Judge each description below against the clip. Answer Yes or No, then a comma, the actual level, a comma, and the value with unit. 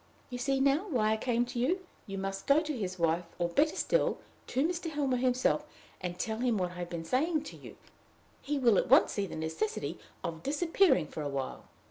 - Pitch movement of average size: No, wide, 8.1 semitones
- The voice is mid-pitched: No, high, 240 Hz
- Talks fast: Yes, fast, 215 wpm